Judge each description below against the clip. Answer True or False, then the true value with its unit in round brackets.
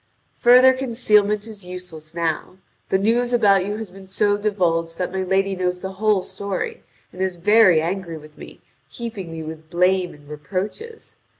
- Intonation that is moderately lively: True (3.6 semitones)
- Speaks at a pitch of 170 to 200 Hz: True (190 Hz)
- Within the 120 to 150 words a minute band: False (170 wpm)